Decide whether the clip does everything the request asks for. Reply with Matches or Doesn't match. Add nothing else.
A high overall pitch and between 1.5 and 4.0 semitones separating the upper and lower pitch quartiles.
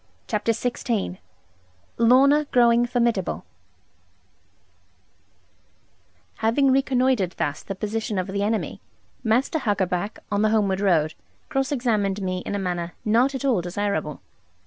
Doesn't match